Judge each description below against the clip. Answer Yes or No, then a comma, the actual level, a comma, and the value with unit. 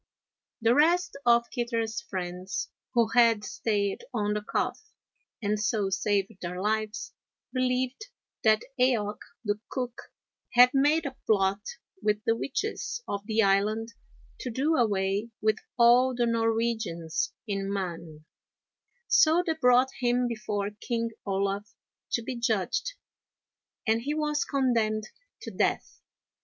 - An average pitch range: Yes, average, 3.4 semitones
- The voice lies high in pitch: Yes, high, 225 Hz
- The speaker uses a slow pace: Yes, slow, 125 wpm